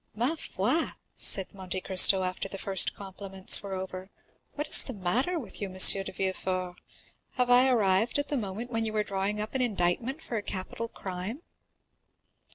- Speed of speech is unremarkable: Yes, average, 175 wpm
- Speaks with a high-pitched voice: Yes, high, 200 Hz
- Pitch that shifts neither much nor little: Yes, average, 4.2 semitones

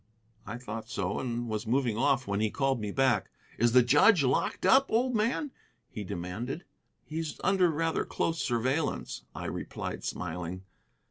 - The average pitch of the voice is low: Yes, low, 125 Hz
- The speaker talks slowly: No, average, 155 wpm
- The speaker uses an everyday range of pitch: No, wide, 6.9 semitones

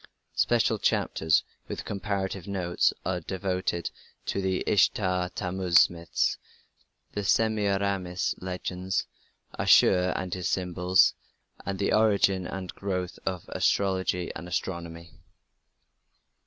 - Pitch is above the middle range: No, very low, 95 Hz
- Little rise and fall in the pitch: Yes, narrow, 1.5 semitones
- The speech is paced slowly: Yes, slow, 100 wpm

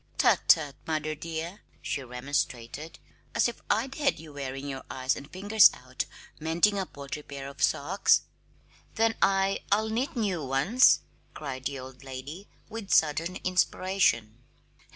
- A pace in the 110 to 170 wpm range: Yes, average, 145 wpm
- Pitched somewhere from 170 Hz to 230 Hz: No, medium, 155 Hz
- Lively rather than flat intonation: Yes, wide, 6.2 semitones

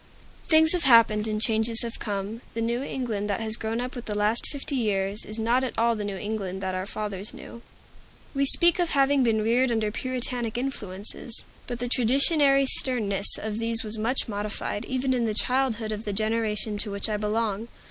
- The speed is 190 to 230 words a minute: Yes, average, 200 wpm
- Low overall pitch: No, high, 225 Hz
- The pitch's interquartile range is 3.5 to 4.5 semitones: No, average, 3.1 semitones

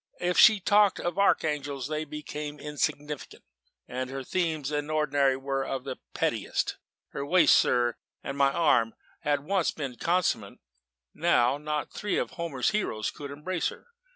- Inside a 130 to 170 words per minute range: Yes, average, 155 wpm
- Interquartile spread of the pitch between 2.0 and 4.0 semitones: Yes, average, 3.6 semitones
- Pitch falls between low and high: Yes, medium, 150 Hz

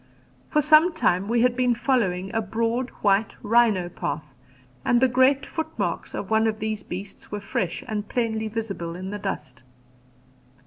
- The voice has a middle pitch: No, high, 220 Hz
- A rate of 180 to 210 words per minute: No, average, 165 wpm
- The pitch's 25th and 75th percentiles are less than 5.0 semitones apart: Yes, average, 3.8 semitones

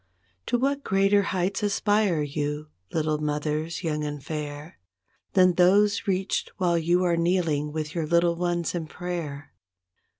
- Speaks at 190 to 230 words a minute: No, average, 140 wpm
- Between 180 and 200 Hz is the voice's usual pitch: No, medium, 170 Hz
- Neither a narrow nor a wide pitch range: Yes, average, 3.6 semitones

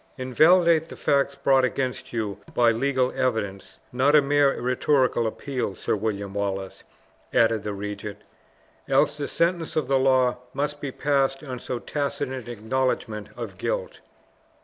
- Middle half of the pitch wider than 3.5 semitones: Yes, average, 4.1 semitones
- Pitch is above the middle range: No, low, 130 Hz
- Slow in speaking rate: No, average, 150 wpm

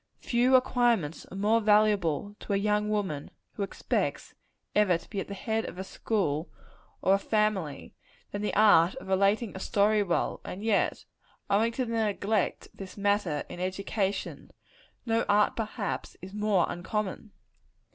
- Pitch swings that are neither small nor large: No, narrow, 2.2 semitones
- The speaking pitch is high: Yes, high, 205 Hz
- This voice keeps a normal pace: Yes, average, 160 wpm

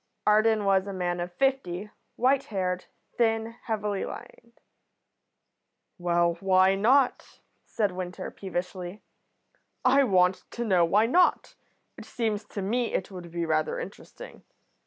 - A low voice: No, high, 195 Hz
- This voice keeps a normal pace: No, slow, 130 wpm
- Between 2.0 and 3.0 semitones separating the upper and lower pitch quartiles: No, average, 3.9 semitones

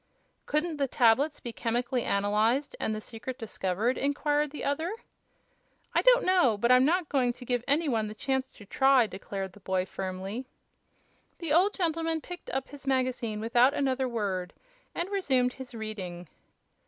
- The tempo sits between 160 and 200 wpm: Yes, average, 165 wpm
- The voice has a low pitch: No, very high, 255 Hz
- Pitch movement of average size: Yes, average, 5.0 semitones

